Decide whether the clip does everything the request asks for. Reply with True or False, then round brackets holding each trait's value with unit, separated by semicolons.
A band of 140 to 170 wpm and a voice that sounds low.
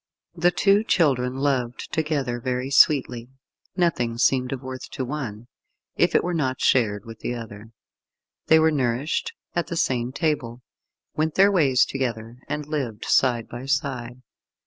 True (150 wpm; 130 Hz)